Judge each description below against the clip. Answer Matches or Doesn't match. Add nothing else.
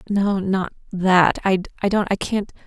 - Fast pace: Doesn't match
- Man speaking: Doesn't match